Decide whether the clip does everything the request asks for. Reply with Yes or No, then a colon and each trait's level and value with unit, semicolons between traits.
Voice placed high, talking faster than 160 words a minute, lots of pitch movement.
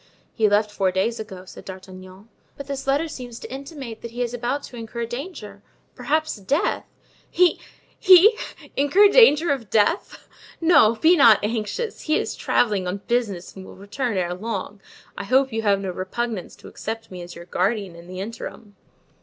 Yes: high, 225 Hz; average, 170 wpm; wide, 5.8 semitones